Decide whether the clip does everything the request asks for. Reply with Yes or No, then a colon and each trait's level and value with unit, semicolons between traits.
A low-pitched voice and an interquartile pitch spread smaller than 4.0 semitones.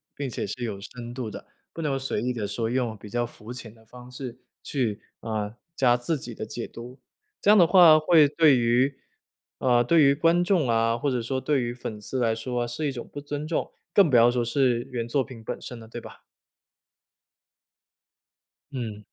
Yes: low, 125 Hz; average, 3.2 semitones